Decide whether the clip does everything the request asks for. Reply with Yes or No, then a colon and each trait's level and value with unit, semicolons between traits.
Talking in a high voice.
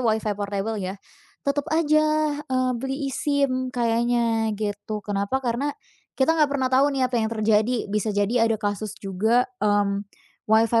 Yes: high, 230 Hz